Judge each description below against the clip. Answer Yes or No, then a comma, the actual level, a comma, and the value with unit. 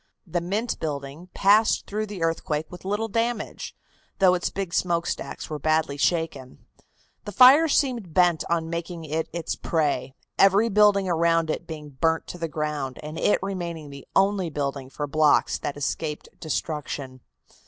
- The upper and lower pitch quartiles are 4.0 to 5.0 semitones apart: Yes, average, 4.4 semitones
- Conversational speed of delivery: Yes, average, 155 wpm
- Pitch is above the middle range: No, medium, 165 Hz